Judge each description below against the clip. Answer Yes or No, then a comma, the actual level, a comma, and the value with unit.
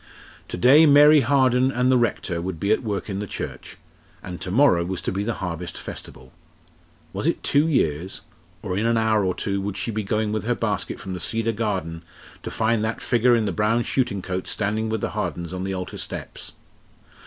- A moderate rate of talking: No, fast, 210 wpm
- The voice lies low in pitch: Yes, low, 105 Hz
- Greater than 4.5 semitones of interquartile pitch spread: No, average, 4.1 semitones